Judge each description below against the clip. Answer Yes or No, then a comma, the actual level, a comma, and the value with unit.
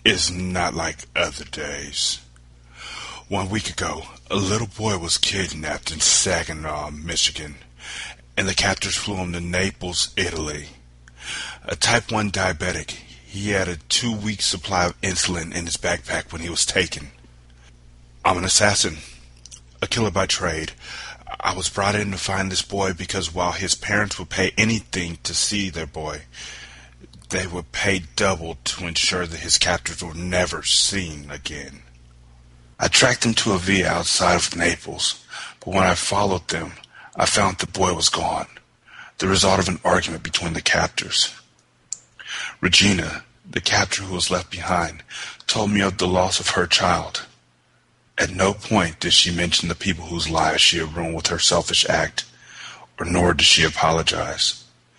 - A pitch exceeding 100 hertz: No, very low, 90 Hz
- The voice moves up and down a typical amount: Yes, average, 4.0 semitones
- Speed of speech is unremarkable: Yes, average, 160 wpm